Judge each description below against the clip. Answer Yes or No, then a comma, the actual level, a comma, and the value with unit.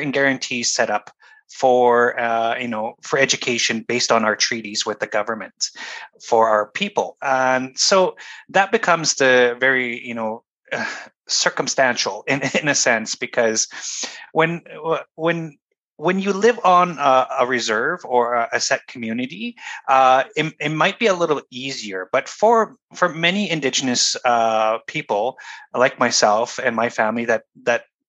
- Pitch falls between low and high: No, low, 130 Hz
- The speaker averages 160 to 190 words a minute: No, average, 145 wpm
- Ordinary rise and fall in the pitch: No, wide, 6.0 semitones